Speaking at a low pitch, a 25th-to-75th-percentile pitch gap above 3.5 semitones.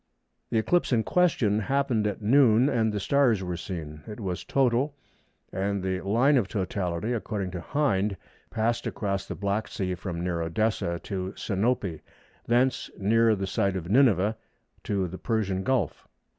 Yes: low, 105 Hz; average, 4.0 semitones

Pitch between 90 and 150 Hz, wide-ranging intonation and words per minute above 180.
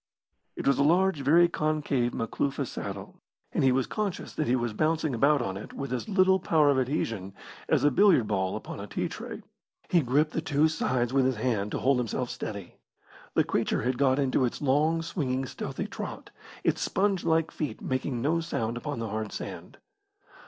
No: low, 135 Hz; average, 4.7 semitones; average, 195 wpm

